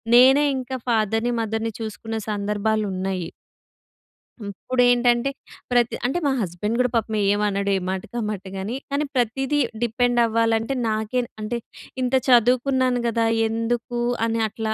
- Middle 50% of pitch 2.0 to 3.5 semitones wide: Yes, narrow, 2.4 semitones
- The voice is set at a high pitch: Yes, high, 230 Hz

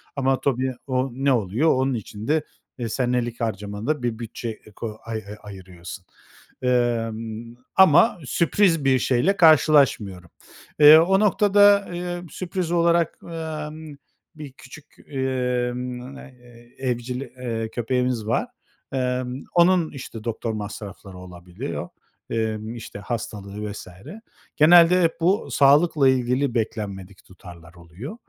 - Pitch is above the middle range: No, low, 125 Hz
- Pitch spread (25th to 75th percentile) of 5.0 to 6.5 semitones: Yes, wide, 5.5 semitones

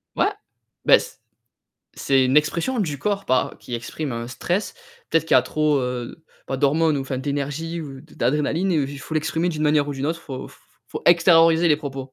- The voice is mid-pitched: Yes, medium, 150 Hz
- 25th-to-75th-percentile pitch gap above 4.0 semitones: No, average, 3.4 semitones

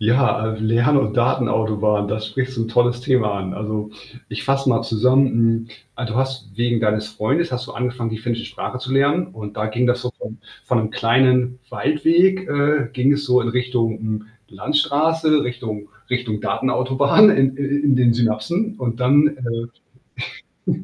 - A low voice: Yes, low, 125 Hz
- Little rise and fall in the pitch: No, average, 3.6 semitones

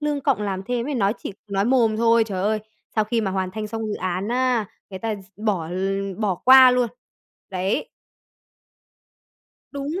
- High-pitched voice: Yes, high, 215 Hz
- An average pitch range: Yes, average, 4.0 semitones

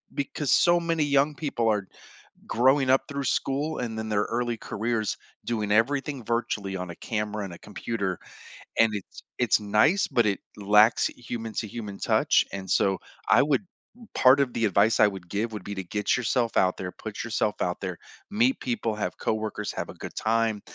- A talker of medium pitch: No, low, 110 Hz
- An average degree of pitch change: Yes, average, 3.9 semitones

